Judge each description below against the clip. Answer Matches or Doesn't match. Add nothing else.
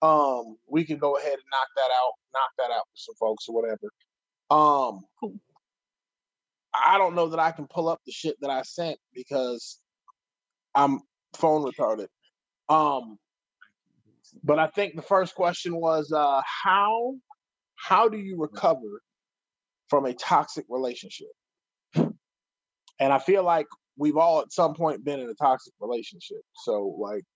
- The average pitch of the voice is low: Doesn't match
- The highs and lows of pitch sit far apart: Matches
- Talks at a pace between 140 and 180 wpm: Matches